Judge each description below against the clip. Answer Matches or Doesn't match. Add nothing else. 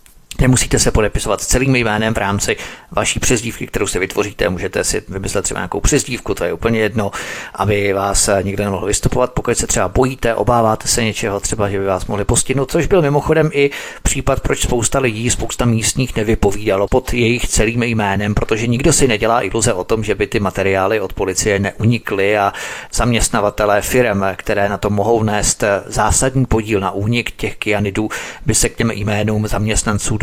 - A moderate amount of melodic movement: Matches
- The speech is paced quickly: Matches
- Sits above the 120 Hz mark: Doesn't match